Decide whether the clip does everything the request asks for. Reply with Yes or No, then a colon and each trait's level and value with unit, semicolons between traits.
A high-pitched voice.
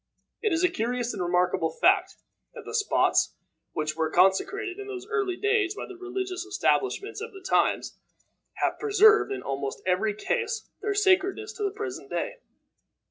Yes: very high, 385 Hz